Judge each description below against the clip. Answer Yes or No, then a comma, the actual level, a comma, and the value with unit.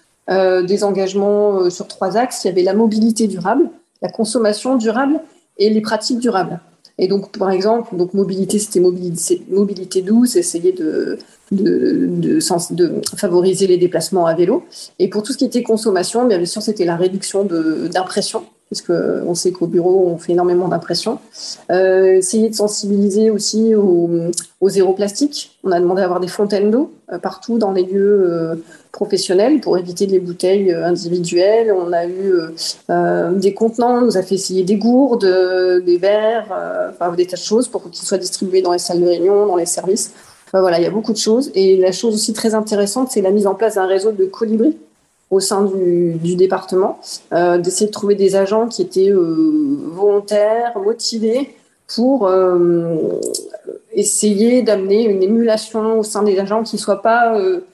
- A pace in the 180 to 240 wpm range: Yes, average, 185 wpm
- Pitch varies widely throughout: No, average, 3.5 semitones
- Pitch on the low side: No, high, 200 Hz